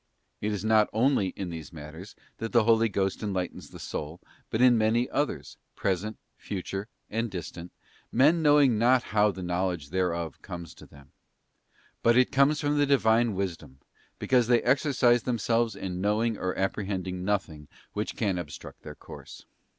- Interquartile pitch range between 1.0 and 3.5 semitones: No, average, 4.7 semitones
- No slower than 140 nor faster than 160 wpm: Yes, average, 150 wpm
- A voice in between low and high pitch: No, low, 105 Hz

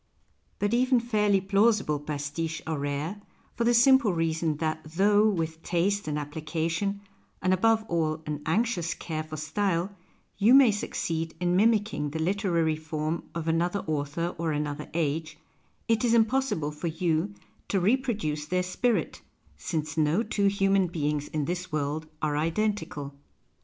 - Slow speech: No, average, 150 wpm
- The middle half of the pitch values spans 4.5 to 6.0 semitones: Yes, average, 4.8 semitones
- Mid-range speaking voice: Yes, medium, 170 Hz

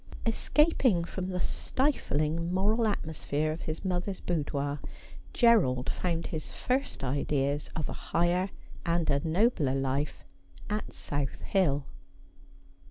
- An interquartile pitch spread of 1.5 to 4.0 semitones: No, average, 5.1 semitones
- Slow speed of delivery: Yes, slow, 115 wpm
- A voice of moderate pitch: Yes, medium, 170 Hz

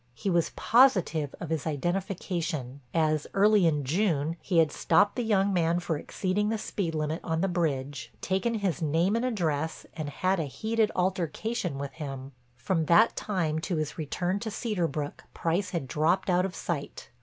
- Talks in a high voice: No, medium, 170 Hz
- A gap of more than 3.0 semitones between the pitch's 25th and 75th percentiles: Yes, average, 4.1 semitones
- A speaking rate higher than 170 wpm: Yes, average, 180 wpm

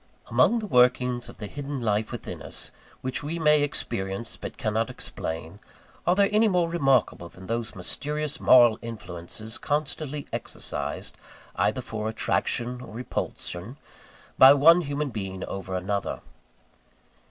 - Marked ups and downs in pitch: Yes, wide, 5.8 semitones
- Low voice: Yes, low, 125 Hz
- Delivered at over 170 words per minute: No, slow, 135 wpm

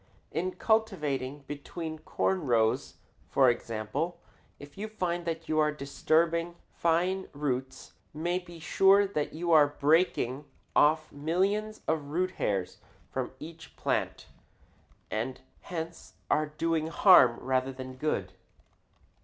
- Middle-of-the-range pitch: Yes, medium, 155 Hz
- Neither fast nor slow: No, slow, 125 wpm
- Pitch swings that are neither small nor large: Yes, average, 3.8 semitones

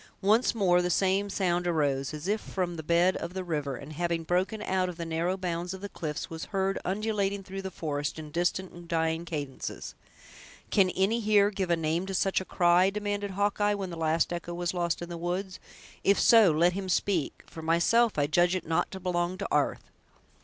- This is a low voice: No, medium, 180 Hz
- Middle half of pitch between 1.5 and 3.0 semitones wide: Yes, narrow, 2.6 semitones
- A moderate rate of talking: No, fast, 210 wpm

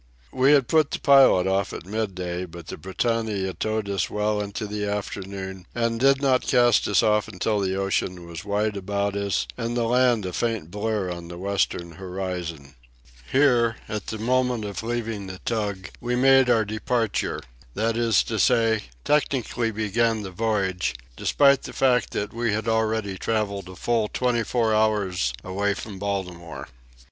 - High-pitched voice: No, low, 105 Hz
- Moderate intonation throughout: Yes, average, 3.5 semitones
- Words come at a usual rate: Yes, average, 165 wpm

